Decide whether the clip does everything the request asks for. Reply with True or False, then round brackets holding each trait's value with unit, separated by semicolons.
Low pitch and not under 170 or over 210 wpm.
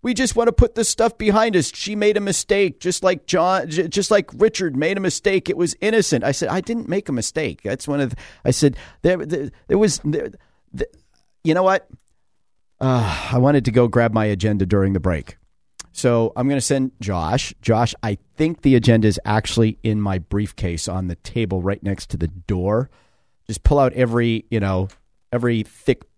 True (125 Hz; 205 wpm)